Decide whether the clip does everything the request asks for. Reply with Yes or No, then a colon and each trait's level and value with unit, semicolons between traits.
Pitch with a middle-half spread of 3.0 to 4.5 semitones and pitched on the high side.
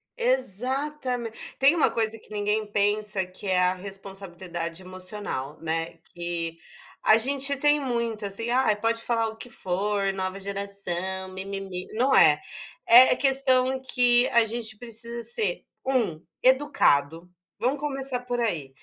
No: average, 5.0 semitones; high, 215 Hz